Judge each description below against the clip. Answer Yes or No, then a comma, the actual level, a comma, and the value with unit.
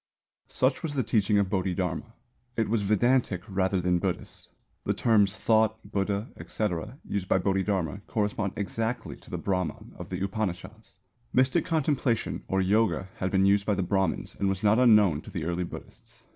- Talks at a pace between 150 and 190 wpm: Yes, average, 170 wpm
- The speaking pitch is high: No, low, 100 Hz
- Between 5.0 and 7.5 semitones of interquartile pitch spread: No, average, 2.8 semitones